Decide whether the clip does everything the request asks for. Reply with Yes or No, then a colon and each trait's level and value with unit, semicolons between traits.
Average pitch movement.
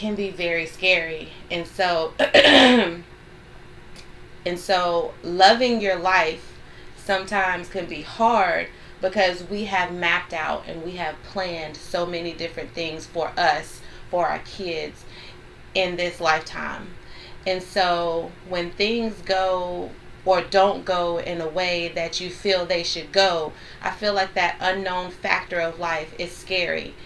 No: narrow, 2.0 semitones